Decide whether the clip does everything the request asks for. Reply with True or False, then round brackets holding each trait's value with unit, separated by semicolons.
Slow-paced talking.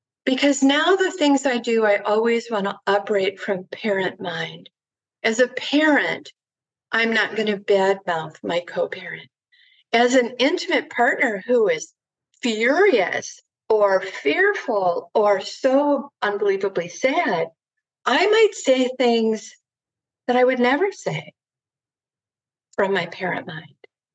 True (125 wpm)